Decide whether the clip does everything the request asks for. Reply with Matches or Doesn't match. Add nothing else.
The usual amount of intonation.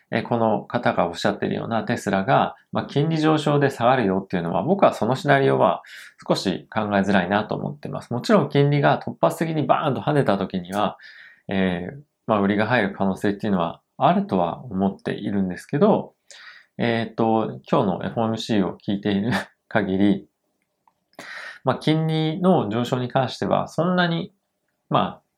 Doesn't match